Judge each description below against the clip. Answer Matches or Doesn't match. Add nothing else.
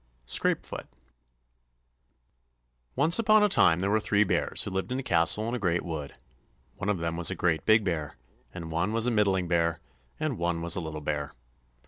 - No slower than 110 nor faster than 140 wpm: Doesn't match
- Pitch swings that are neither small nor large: Matches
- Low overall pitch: Matches